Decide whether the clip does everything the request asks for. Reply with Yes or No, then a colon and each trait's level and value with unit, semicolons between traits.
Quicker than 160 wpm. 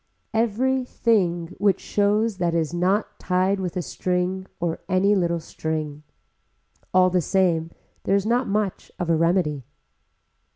No: average, 140 wpm